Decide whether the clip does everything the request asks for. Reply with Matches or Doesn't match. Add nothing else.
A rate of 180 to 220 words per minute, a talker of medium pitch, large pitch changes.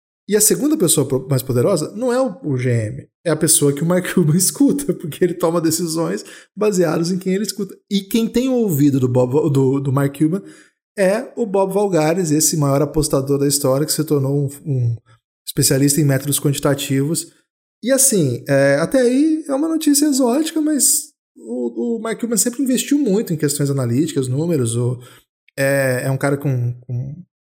Matches